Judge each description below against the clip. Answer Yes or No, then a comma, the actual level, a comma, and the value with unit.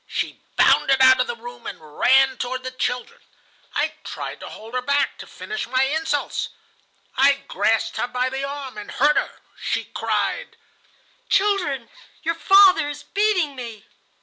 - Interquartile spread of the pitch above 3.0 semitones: Yes, average, 4.2 semitones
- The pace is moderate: Yes, average, 160 wpm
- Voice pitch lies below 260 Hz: No, very high, 270 Hz